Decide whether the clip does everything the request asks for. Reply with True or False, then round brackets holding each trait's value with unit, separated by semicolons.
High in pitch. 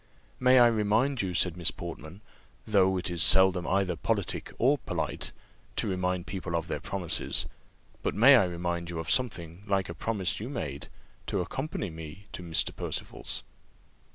False (95 Hz)